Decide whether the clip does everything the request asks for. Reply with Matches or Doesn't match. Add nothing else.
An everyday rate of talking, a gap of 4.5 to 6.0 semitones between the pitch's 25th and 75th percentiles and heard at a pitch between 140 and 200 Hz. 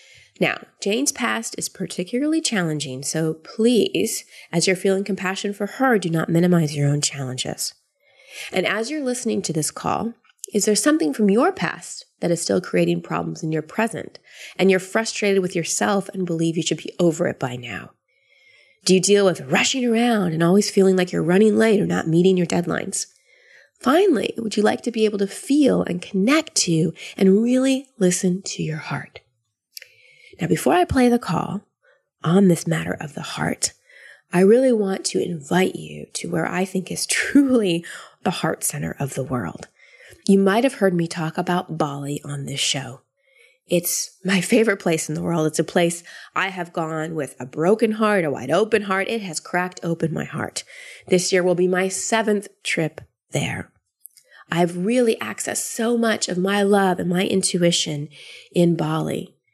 Matches